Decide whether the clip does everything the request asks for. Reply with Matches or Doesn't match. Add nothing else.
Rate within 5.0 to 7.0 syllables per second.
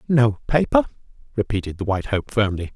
Matches